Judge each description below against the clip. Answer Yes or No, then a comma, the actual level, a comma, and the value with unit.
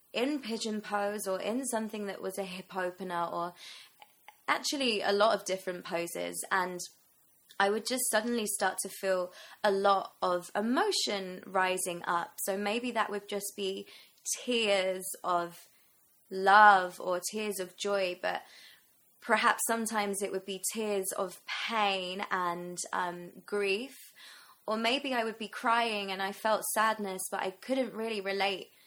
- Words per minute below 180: Yes, average, 150 wpm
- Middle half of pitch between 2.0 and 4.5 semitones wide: Yes, narrow, 2.6 semitones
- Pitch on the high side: Yes, high, 200 Hz